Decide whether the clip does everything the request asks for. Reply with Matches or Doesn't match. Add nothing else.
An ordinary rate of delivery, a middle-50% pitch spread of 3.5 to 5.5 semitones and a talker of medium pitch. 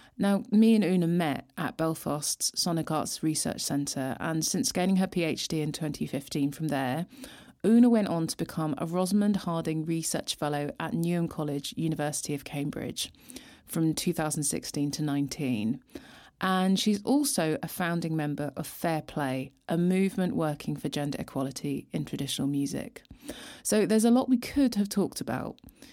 Matches